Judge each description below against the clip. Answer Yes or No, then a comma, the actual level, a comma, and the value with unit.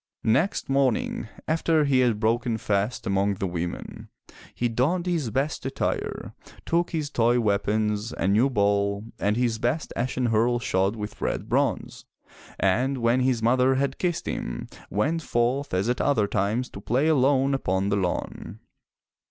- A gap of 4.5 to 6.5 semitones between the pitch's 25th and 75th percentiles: Yes, average, 4.8 semitones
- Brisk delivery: No, average, 155 wpm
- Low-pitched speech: Yes, low, 120 Hz